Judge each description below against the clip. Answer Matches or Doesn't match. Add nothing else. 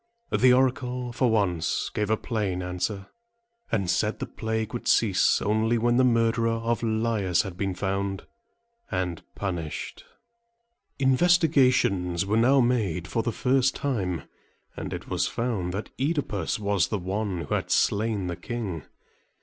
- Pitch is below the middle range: Matches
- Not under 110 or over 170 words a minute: Matches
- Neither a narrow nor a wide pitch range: Matches